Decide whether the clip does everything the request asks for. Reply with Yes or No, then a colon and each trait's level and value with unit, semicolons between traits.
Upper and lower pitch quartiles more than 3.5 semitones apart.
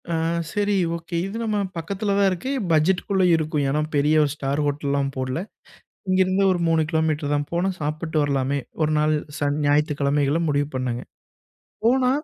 Yes: average, 4.3 semitones